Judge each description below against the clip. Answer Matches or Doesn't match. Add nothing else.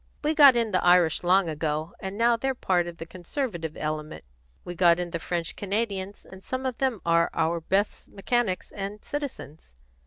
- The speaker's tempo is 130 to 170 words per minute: Doesn't match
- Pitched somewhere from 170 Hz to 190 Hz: Matches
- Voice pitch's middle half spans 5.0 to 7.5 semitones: Matches